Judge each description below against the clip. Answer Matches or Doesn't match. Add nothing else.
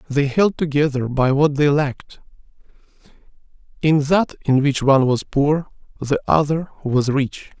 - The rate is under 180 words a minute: Matches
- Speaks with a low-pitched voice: Doesn't match